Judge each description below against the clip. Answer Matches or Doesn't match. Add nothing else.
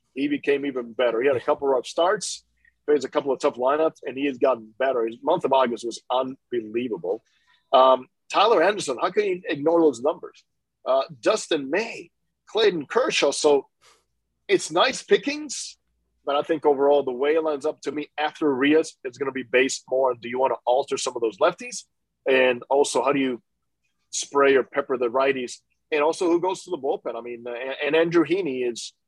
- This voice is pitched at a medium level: Matches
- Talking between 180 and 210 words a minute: Matches